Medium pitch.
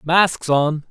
Yes: medium, 160 Hz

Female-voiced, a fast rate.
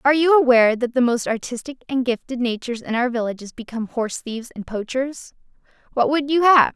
No: female; average, 195 wpm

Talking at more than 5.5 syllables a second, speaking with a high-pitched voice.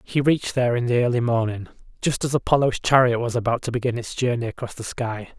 No: 6.3 syllables/s; low, 120 Hz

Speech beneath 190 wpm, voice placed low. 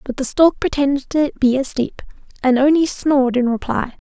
No: average, 175 wpm; very high, 270 Hz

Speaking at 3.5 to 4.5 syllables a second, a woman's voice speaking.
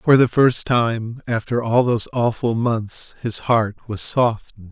No: 4.0 syllables/s; male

